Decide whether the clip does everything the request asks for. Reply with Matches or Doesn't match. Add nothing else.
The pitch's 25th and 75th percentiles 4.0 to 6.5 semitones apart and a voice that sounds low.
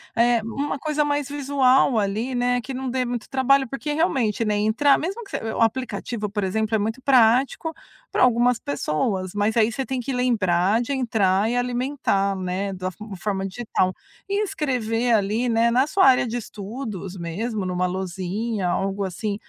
Doesn't match